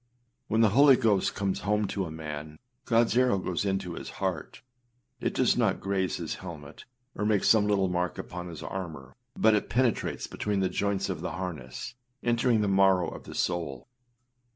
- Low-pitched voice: Yes, very low, 95 Hz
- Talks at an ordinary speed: Yes, average, 180 wpm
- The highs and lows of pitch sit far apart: No, average, 3.4 semitones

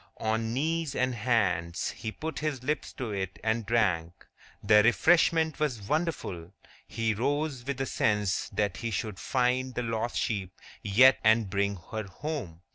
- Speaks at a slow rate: No, average, 155 wpm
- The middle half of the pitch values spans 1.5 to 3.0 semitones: No, average, 4.6 semitones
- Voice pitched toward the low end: Yes, low, 115 Hz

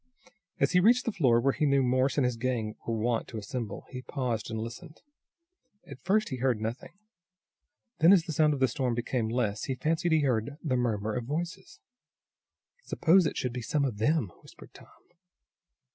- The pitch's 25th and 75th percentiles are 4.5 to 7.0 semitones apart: Yes, average, 5.0 semitones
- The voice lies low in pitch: Yes, low, 130 Hz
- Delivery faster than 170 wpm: Yes, average, 190 wpm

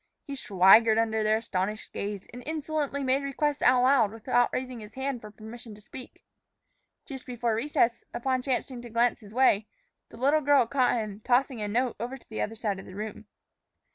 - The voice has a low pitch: No, high, 240 Hz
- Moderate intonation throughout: Yes, average, 3.4 semitones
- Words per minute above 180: Yes, average, 190 wpm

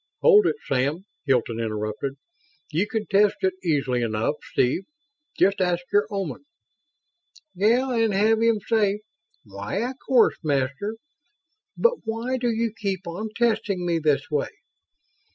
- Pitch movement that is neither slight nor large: No, wide, 7.7 semitones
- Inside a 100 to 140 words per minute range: Yes, slow, 135 wpm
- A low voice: No, high, 195 Hz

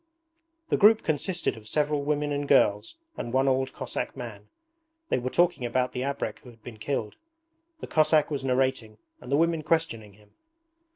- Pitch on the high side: No, low, 135 Hz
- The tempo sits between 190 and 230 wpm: No, average, 175 wpm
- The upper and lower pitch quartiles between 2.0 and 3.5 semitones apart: No, average, 4.3 semitones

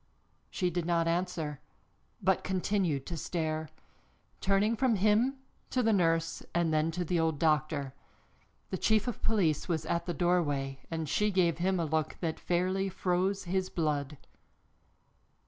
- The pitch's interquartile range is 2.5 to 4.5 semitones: Yes, average, 3.2 semitones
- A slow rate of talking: No, average, 150 wpm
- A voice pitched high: No, medium, 175 Hz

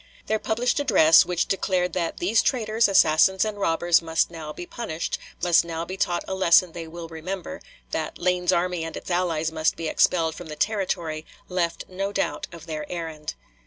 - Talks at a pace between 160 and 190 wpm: Yes, average, 185 wpm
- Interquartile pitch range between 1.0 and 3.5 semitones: Yes, average, 2.7 semitones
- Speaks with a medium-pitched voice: Yes, medium, 175 Hz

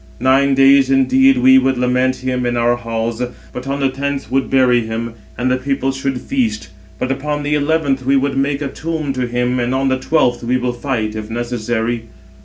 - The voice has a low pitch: Yes, low, 130 Hz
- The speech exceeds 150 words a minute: Yes, fast, 205 wpm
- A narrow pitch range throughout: Yes, narrow, 2.3 semitones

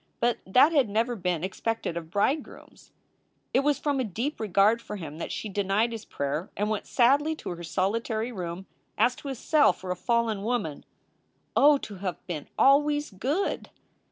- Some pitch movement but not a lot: No, wide, 5.9 semitones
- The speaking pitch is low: No, high, 220 Hz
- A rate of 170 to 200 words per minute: Yes, average, 180 wpm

